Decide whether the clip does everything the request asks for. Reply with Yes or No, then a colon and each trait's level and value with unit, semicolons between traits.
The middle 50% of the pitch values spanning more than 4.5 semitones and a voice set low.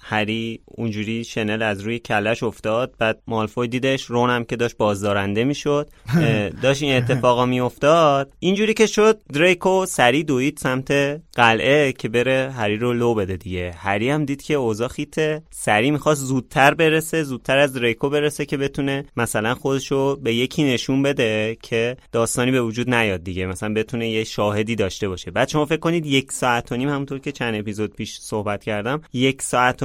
No: average, 4.1 semitones; low, 125 Hz